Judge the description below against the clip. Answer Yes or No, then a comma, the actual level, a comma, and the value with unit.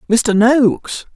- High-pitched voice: Yes, high, 235 Hz